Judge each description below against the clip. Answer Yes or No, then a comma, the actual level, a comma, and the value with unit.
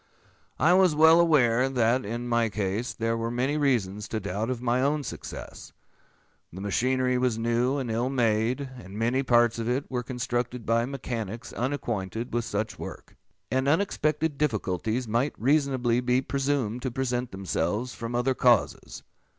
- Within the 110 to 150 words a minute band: No, average, 160 wpm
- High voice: No, low, 120 Hz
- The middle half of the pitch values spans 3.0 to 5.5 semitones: No, narrow, 2.6 semitones